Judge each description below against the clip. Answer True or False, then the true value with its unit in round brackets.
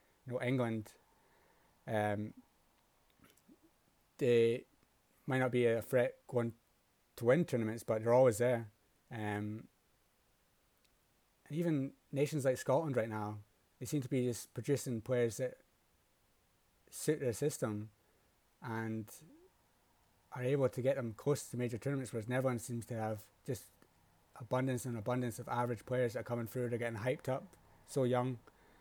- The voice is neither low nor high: False (120 Hz)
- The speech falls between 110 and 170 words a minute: True (145 wpm)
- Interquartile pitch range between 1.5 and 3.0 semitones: True (2.7 semitones)